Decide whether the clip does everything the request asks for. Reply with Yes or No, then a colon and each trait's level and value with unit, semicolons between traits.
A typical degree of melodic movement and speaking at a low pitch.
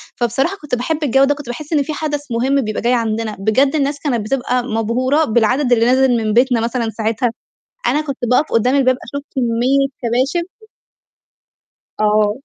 No: average, 3.4 semitones; very high, 250 Hz